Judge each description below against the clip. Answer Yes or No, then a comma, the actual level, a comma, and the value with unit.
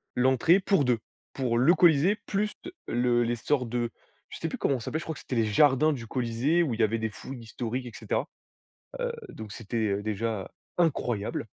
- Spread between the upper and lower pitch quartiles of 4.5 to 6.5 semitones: Yes, average, 5.0 semitones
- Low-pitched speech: Yes, low, 125 Hz